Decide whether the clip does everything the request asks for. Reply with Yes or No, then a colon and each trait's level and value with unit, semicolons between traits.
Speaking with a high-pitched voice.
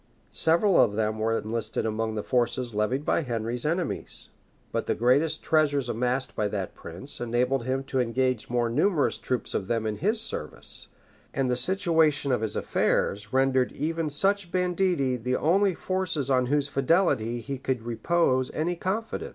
No: low, 130 Hz